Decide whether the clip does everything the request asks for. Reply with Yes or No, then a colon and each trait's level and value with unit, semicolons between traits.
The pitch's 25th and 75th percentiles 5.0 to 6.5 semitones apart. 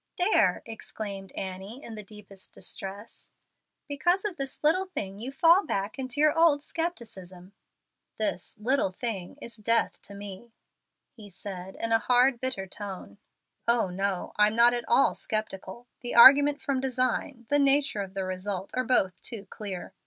Yes: wide, 5.5 semitones